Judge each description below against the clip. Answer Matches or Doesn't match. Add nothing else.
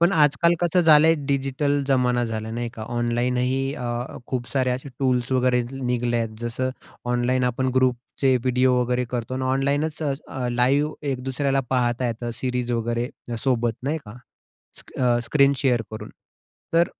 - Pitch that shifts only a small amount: Matches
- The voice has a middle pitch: Doesn't match